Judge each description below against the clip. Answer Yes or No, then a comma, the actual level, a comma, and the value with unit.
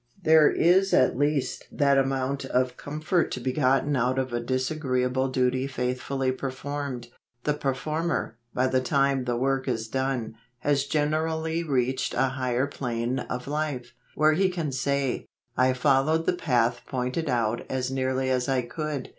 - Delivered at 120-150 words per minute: No, average, 165 wpm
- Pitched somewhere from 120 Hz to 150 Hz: Yes, low, 135 Hz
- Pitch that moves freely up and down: No, narrow, 2.5 semitones